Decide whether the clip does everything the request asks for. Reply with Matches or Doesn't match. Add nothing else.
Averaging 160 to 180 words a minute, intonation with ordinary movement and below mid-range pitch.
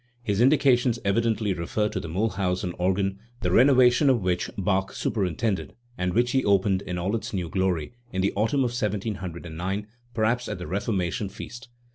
Matches